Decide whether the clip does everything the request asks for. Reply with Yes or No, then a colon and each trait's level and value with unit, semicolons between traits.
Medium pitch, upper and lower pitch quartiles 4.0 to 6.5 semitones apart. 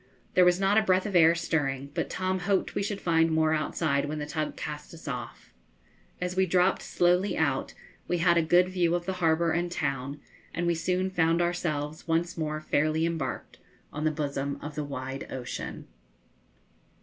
No: medium, 165 Hz; average, 2.9 semitones